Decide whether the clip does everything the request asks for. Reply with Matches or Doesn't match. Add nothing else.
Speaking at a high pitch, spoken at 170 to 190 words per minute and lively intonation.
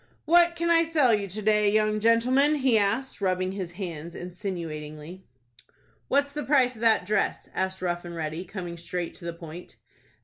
Matches